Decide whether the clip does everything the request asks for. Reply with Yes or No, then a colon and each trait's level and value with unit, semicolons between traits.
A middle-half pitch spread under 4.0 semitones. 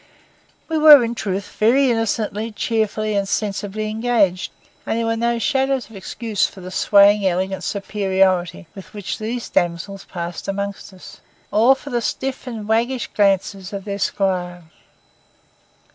Yes: average, 3.1 semitones